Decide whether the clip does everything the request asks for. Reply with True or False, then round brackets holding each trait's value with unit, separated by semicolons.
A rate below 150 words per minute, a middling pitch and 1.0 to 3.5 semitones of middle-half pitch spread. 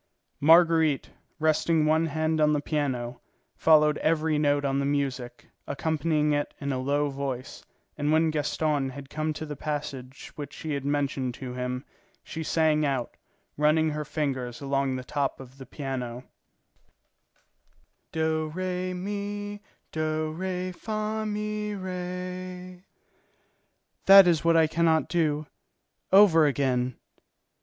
True (135 wpm; 155 Hz; 3.1 semitones)